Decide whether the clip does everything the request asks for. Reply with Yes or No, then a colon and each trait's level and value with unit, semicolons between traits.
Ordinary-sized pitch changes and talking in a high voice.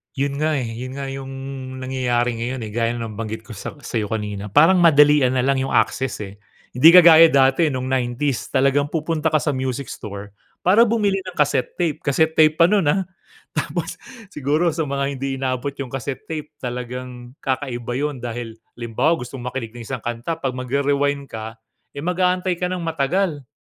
No: average, 4.0 semitones; low, 135 Hz